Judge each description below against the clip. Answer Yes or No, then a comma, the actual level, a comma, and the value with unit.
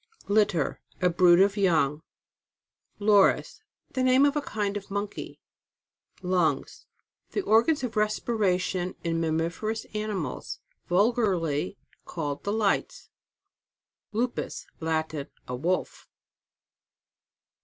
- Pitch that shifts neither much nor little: Yes, average, 4.3 semitones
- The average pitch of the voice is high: Yes, high, 195 Hz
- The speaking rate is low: Yes, slow, 100 wpm